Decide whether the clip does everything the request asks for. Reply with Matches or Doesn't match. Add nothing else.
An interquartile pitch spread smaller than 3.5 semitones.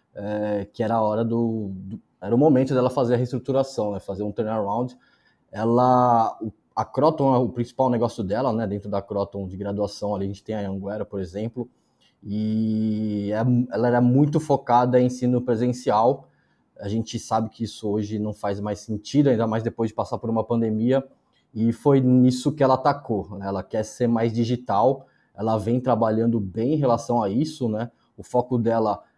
Matches